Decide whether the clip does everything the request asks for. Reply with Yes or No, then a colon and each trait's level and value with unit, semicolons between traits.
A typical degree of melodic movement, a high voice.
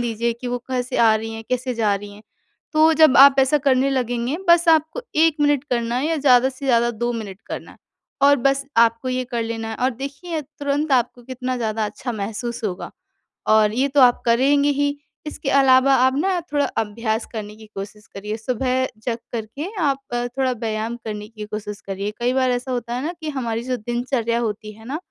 Yes: average, 3.5 semitones; high, 245 Hz